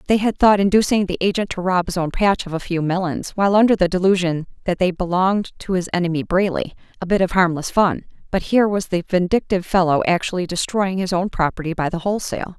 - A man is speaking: No, female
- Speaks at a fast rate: Yes, fast, 215 wpm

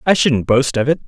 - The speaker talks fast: Yes, fast, 280 wpm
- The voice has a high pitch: No, low, 135 Hz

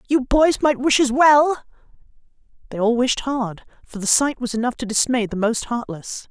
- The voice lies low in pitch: No, very high, 250 Hz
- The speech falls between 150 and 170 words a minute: No, average, 190 wpm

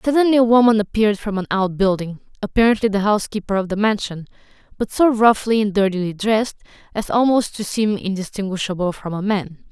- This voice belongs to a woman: Yes, female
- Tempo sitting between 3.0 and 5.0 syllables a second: No, 6.0 syllables/s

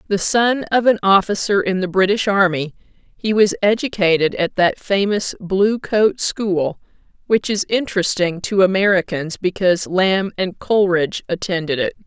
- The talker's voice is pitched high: Yes, high, 195 Hz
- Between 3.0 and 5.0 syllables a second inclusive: Yes, 4.6 syllables/s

